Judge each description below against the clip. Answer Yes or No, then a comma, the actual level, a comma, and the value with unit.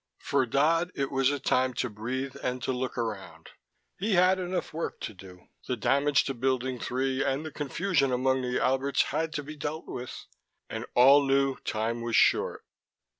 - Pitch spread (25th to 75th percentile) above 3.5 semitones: No, average, 2.8 semitones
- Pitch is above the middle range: No, low, 135 Hz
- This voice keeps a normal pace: Yes, average, 180 wpm